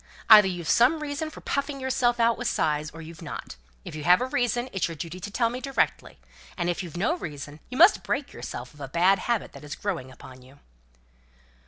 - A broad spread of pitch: Yes, wide, 8.3 semitones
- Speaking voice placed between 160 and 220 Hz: Yes, high, 190 Hz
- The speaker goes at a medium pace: No, fast, 230 wpm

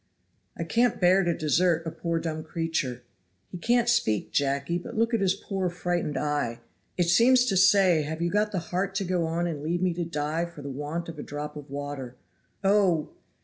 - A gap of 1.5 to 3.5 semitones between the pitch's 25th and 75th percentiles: No, average, 3.9 semitones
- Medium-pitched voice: Yes, medium, 170 Hz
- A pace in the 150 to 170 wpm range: No, fast, 205 wpm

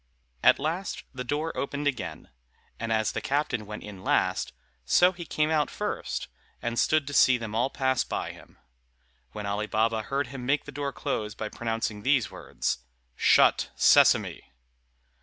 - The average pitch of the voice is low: Yes, low, 130 Hz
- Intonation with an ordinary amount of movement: Yes, average, 4.9 semitones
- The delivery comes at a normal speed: Yes, average, 165 wpm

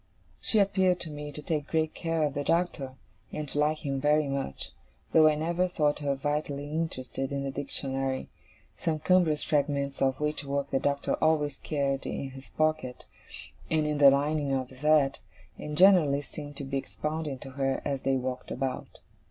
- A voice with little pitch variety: Yes, narrow, 2.2 semitones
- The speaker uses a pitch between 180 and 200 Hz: No, medium, 145 Hz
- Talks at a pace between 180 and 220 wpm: Yes, average, 185 wpm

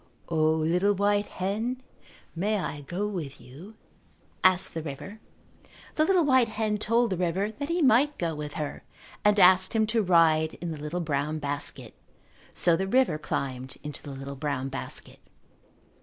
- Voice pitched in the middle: Yes, medium, 180 Hz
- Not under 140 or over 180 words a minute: Yes, average, 165 wpm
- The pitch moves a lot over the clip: Yes, wide, 5.9 semitones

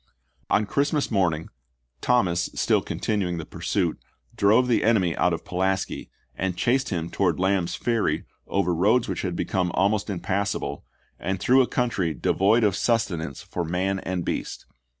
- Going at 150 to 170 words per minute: Yes, average, 165 wpm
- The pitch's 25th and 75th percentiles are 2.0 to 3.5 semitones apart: No, average, 3.9 semitones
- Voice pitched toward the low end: Yes, very low, 95 Hz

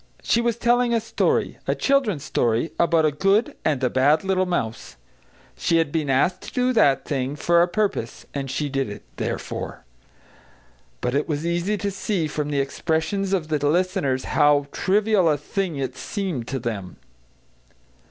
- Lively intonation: Yes, wide, 5.8 semitones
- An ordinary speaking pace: Yes, average, 170 wpm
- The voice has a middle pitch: Yes, medium, 160 Hz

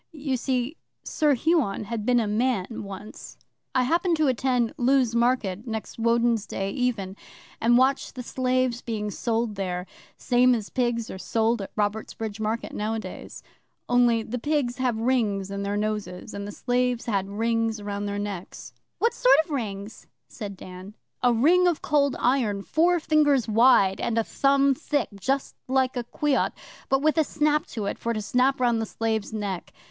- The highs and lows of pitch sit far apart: No, average, 3.8 semitones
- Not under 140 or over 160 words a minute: No, average, 175 wpm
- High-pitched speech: Yes, high, 235 Hz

